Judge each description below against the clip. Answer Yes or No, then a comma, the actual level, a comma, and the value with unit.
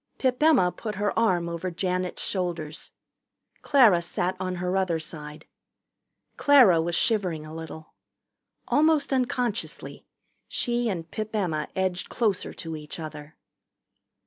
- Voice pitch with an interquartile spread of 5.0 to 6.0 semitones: Yes, average, 5.3 semitones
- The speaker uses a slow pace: Yes, slow, 125 wpm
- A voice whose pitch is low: No, medium, 185 Hz